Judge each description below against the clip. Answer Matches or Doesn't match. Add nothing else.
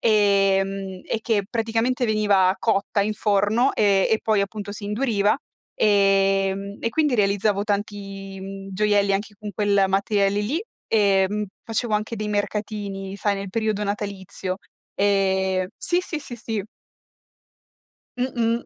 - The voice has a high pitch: Matches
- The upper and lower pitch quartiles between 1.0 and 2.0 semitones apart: Matches